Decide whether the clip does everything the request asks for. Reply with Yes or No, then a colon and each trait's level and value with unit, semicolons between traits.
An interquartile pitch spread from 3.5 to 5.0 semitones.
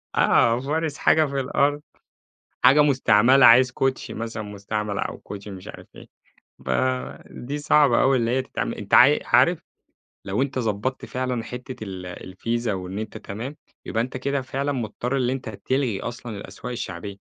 Yes: average, 3.9 semitones